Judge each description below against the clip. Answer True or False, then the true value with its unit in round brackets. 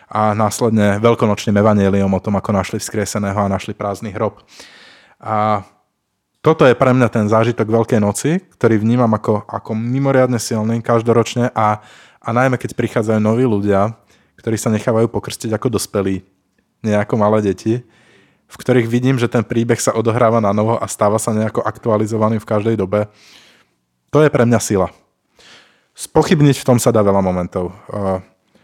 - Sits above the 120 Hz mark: False (110 Hz)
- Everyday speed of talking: True (155 wpm)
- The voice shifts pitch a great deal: False (2.4 semitones)